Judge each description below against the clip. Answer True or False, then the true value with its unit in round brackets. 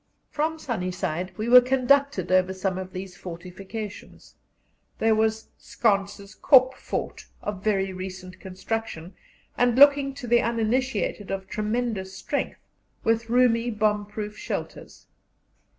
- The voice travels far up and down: False (4.2 semitones)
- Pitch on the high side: True (215 Hz)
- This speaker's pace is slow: True (125 wpm)